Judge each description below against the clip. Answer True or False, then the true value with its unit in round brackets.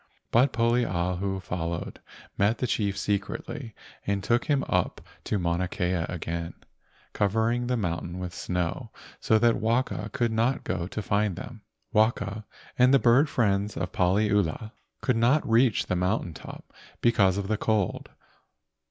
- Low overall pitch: True (105 Hz)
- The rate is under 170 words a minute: True (145 wpm)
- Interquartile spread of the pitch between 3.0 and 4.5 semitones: True (4.2 semitones)